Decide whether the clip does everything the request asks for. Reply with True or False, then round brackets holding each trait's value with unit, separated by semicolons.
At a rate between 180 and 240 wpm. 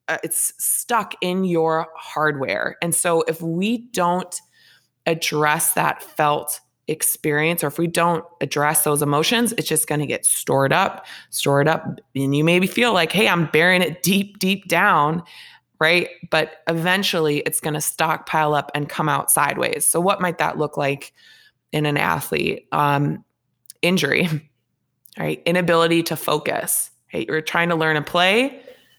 False (160 wpm)